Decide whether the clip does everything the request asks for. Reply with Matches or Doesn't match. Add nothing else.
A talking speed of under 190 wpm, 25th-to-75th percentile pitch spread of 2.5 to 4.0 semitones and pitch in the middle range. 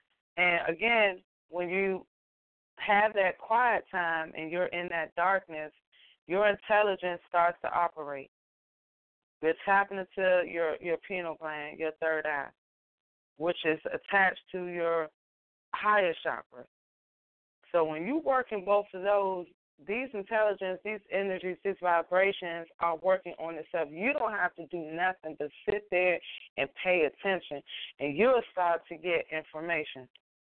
Matches